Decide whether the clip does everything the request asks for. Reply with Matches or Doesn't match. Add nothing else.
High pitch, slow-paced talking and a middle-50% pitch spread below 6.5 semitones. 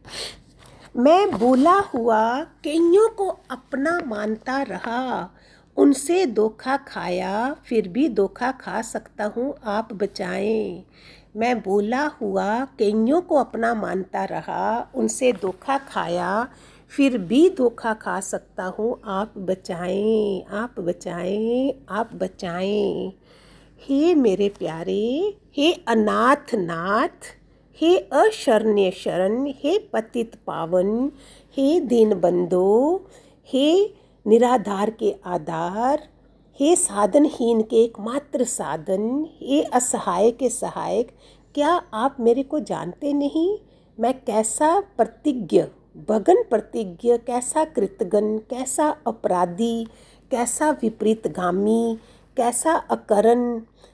Matches